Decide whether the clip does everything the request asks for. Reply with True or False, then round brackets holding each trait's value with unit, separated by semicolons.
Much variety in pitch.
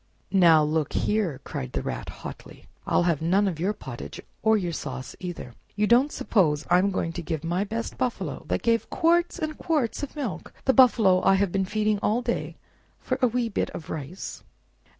True (5.8 semitones)